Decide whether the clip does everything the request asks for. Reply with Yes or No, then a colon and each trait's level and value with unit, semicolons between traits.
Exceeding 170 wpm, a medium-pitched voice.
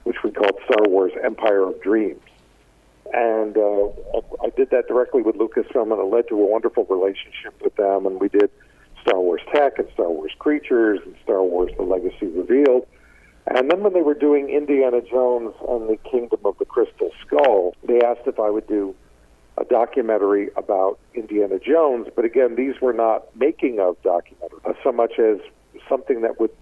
Yes: average, 185 wpm; medium, 145 Hz